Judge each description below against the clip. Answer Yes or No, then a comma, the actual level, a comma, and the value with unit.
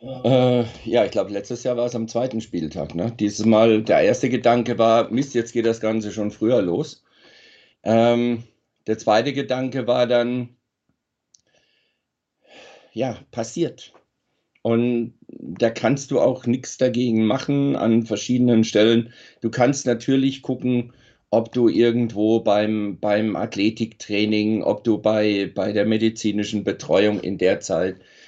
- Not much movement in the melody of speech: Yes, narrow, 2.3 semitones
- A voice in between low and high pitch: No, low, 115 Hz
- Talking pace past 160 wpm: No, average, 135 wpm